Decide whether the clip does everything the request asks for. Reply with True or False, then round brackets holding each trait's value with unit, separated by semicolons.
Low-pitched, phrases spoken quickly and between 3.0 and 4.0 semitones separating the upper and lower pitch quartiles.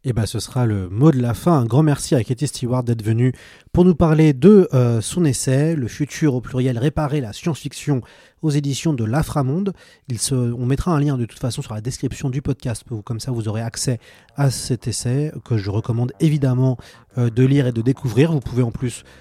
True (130 Hz; 225 wpm; 3.7 semitones)